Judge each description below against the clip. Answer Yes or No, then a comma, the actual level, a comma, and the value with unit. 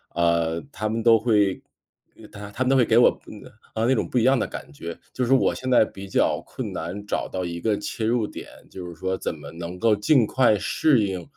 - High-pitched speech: No, low, 105 Hz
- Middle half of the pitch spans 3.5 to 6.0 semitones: Yes, average, 4.4 semitones